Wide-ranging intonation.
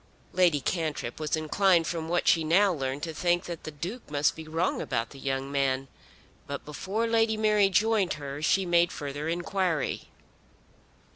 No: average, 4.4 semitones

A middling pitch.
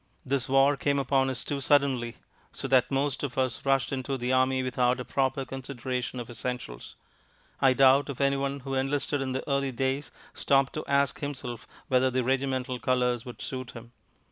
No: low, 130 Hz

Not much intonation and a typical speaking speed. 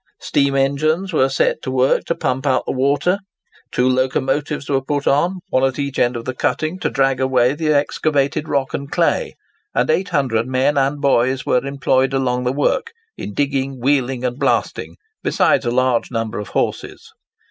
Yes: narrow, 1.9 semitones; average, 180 wpm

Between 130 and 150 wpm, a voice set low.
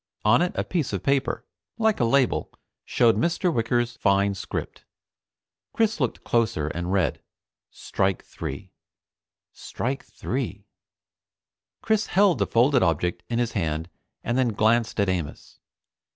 Yes: slow, 135 wpm; low, 115 Hz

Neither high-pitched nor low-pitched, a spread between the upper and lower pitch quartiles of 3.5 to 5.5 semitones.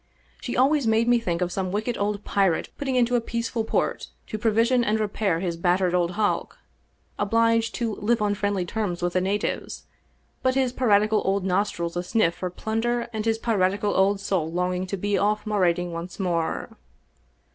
No: high, 205 Hz; average, 3.8 semitones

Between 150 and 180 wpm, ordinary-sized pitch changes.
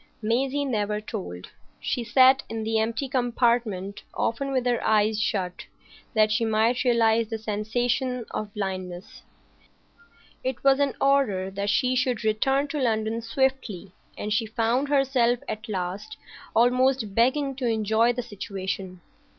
No: average, 140 wpm; average, 3.3 semitones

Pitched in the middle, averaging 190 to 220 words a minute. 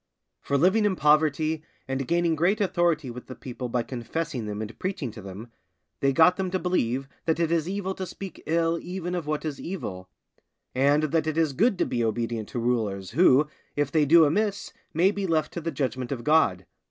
Yes: medium, 155 Hz; fast, 205 wpm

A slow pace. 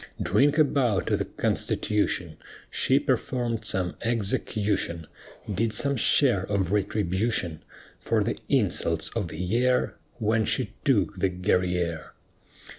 Yes: slow, 120 wpm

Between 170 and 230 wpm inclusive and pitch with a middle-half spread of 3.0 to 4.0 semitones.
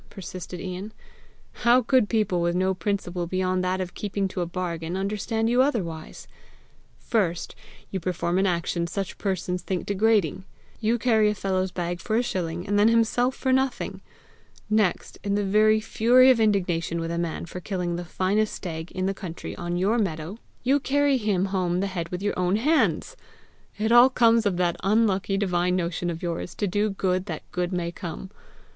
Yes: average, 185 wpm; average, 3.6 semitones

